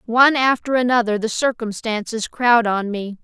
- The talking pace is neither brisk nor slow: Yes, average, 150 wpm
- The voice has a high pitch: Yes, high, 230 Hz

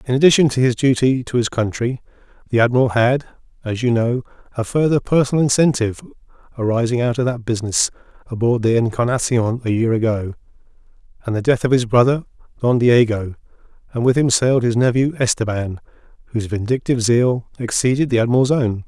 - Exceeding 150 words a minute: Yes, average, 160 wpm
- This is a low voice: Yes, low, 120 Hz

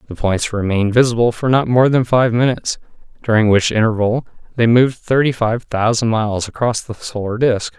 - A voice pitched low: Yes, low, 115 Hz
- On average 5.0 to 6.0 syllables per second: Yes, 5.6 syllables/s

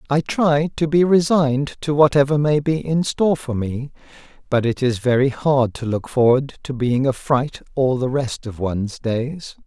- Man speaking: Yes, male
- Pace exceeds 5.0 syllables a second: No, 4.6 syllables/s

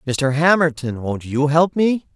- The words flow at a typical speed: Yes, average, 165 wpm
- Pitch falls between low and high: Yes, medium, 150 Hz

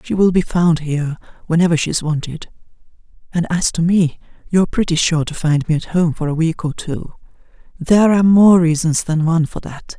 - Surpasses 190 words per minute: Yes, average, 200 wpm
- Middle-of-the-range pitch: Yes, medium, 165 Hz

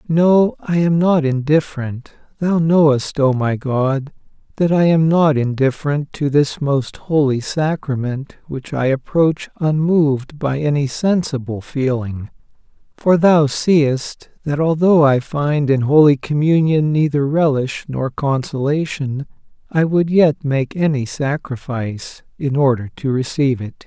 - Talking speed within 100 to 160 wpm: Yes, slow, 135 wpm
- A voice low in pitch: No, medium, 145 Hz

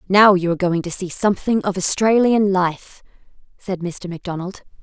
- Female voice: Yes, female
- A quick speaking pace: No, average, 160 wpm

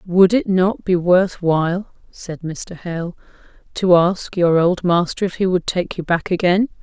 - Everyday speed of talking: Yes, average, 185 wpm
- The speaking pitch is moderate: Yes, medium, 180 Hz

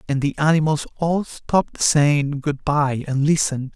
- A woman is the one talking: No, male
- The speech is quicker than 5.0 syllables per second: No, 4.3 syllables/s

